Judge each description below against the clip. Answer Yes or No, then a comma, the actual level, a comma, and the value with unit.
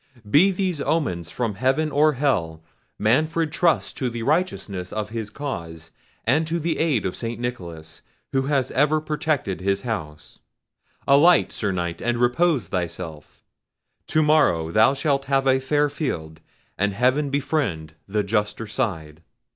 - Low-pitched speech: Yes, low, 125 Hz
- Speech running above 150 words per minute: No, average, 145 wpm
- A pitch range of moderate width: No, wide, 8.1 semitones